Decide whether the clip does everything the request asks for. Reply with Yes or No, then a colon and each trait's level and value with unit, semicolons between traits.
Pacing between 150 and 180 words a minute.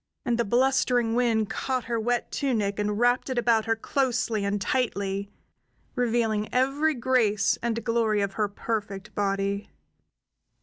No: average, 140 wpm